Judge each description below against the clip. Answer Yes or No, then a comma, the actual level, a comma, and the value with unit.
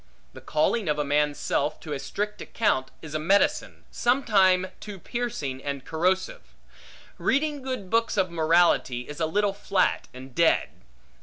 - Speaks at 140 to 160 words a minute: Yes, average, 155 wpm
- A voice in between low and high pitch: Yes, medium, 175 Hz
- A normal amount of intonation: No, wide, 5.8 semitones